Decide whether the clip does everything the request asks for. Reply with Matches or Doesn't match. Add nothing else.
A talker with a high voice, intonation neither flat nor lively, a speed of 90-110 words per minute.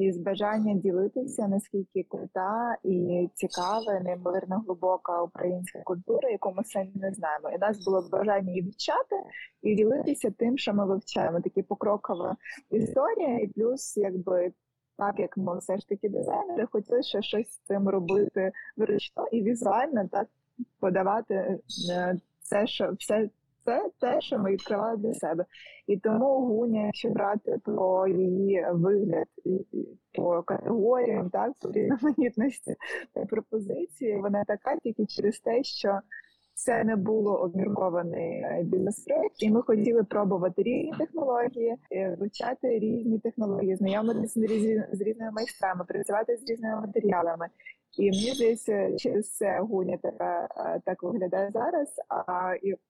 Doesn't match